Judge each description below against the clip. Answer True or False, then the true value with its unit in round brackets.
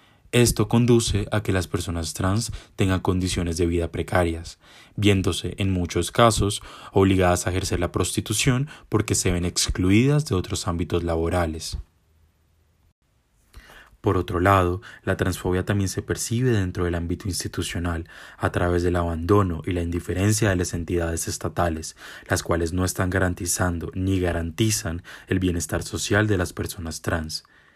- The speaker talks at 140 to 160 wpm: True (145 wpm)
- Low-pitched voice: True (90 Hz)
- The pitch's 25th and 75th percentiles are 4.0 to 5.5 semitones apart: False (3.0 semitones)